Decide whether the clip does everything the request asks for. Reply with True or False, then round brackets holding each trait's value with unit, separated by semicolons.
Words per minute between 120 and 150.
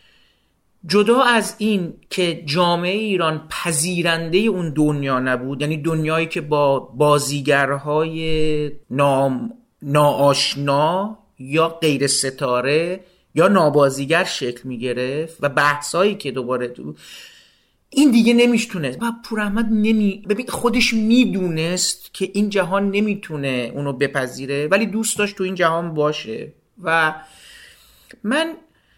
False (110 wpm)